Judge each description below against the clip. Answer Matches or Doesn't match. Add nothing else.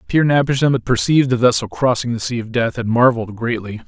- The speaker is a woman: Doesn't match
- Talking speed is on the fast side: Matches